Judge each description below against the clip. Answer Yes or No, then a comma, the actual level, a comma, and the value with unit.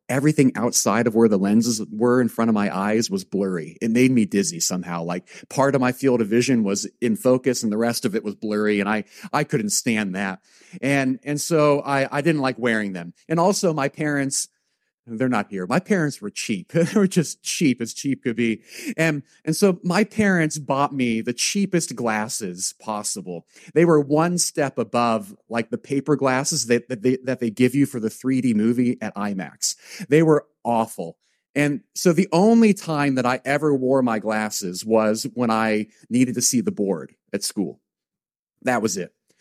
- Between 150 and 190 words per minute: No, average, 200 wpm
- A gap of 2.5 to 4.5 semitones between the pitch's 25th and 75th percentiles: No, average, 5.2 semitones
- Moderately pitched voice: No, low, 125 Hz